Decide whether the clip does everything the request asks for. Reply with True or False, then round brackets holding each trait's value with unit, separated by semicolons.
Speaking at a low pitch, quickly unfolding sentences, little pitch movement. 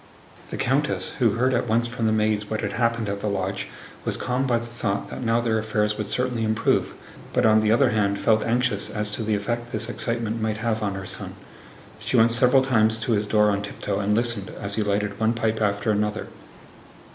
True (110 Hz; 220 wpm; 2.0 semitones)